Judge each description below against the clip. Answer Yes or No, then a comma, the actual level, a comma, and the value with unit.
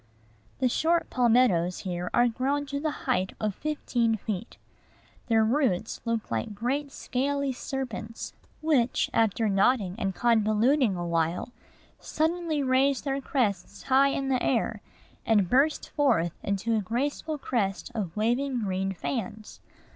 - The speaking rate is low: Yes, slow, 130 wpm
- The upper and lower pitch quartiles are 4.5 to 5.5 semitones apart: Yes, average, 5.2 semitones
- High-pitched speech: Yes, high, 235 Hz